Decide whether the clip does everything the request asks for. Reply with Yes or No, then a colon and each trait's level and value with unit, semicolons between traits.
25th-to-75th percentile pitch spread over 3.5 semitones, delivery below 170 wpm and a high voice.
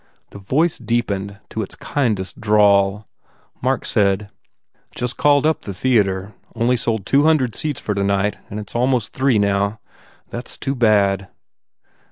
No: average, 3.9 semitones; average, 150 wpm; low, 105 Hz